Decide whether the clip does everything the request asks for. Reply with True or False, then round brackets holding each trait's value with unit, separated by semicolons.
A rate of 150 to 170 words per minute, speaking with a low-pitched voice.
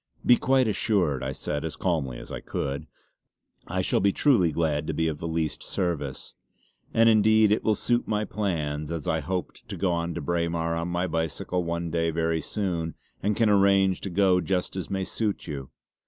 False (200 wpm; 85 Hz)